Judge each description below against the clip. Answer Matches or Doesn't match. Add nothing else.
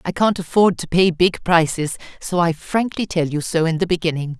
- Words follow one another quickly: Matches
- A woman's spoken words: Matches